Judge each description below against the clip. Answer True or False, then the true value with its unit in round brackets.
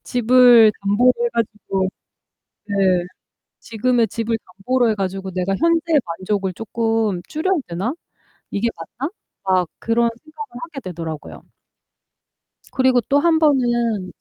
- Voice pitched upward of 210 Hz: True (230 Hz)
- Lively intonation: False (4.7 semitones)